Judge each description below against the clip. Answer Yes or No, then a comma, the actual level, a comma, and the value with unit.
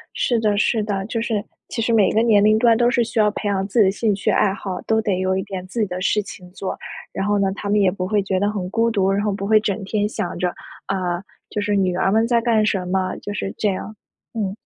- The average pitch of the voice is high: Yes, high, 205 Hz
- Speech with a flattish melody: Yes, narrow, 2.2 semitones